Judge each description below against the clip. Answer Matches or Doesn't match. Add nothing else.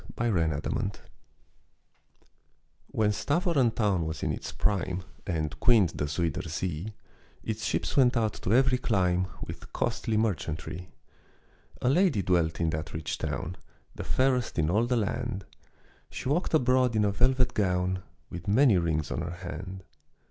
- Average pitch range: Doesn't match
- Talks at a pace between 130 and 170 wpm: Matches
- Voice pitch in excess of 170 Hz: Doesn't match